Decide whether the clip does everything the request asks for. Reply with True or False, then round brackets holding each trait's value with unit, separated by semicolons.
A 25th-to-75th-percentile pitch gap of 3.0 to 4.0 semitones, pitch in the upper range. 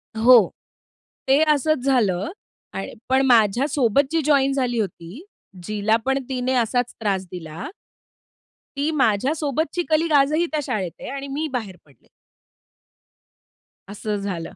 False (5.3 semitones; 255 Hz)